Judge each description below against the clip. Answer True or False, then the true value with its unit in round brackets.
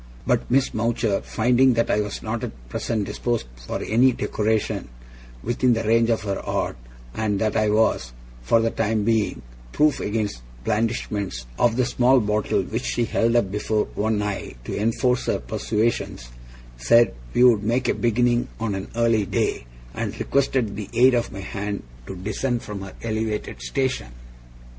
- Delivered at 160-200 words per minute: True (170 wpm)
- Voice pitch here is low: True (110 Hz)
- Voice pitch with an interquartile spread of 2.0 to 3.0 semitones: True (2.5 semitones)